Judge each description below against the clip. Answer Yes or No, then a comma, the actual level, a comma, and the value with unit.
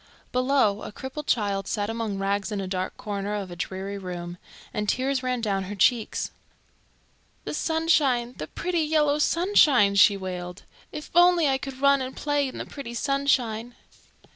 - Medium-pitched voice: No, high, 235 Hz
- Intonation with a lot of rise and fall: Yes, wide, 5.8 semitones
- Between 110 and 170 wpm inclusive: Yes, average, 165 wpm